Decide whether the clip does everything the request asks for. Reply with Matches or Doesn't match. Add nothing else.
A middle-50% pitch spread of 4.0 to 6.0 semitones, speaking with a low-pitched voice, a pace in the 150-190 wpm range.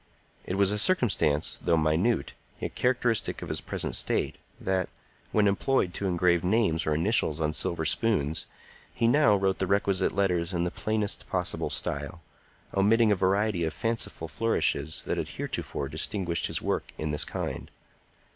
Matches